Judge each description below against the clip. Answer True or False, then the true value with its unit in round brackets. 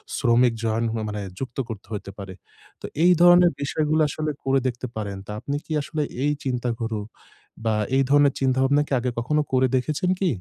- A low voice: True (130 Hz)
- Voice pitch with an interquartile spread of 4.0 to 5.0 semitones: True (4.4 semitones)